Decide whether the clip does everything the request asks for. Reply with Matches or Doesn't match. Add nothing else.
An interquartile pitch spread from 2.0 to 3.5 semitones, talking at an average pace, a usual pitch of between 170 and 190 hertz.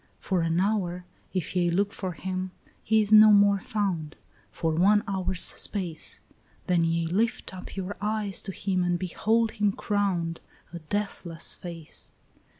Matches